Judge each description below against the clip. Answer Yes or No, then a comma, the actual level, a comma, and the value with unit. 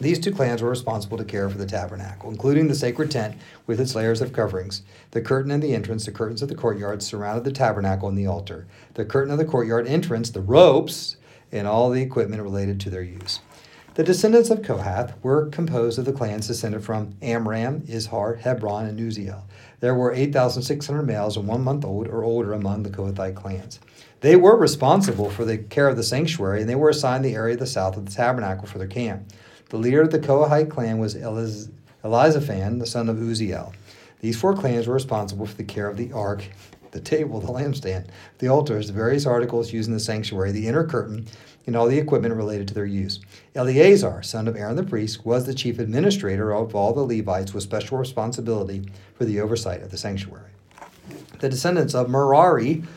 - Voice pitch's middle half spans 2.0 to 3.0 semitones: No, average, 4.2 semitones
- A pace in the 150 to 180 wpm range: No, fast, 205 wpm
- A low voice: Yes, low, 115 Hz